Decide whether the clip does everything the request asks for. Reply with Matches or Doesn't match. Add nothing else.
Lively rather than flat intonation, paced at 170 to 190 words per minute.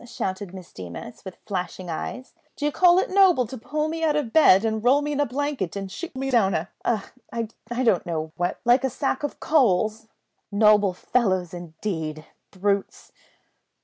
Matches